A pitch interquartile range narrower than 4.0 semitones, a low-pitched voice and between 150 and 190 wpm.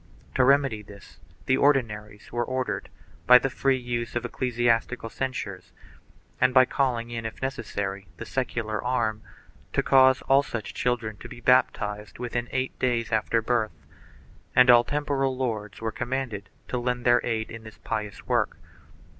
Yes: average, 2.8 semitones; low, 120 Hz; average, 155 wpm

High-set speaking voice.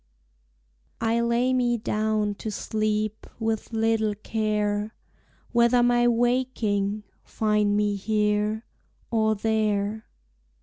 Yes: high, 220 Hz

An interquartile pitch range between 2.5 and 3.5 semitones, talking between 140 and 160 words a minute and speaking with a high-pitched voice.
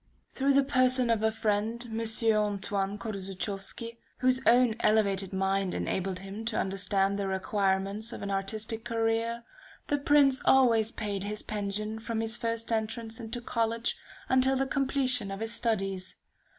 Yes: average, 2.9 semitones; average, 150 wpm; high, 220 Hz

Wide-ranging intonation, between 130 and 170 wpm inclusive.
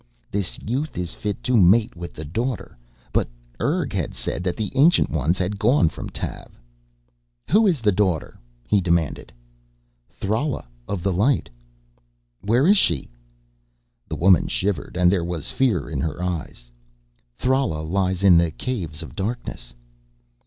Yes: wide, 5.9 semitones; average, 150 wpm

